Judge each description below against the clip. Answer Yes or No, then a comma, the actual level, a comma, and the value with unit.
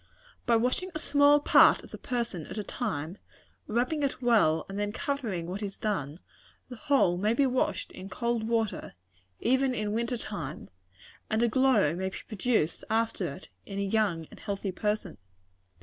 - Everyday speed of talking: Yes, average, 175 wpm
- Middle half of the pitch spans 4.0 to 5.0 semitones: Yes, average, 4.4 semitones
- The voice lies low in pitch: No, high, 220 Hz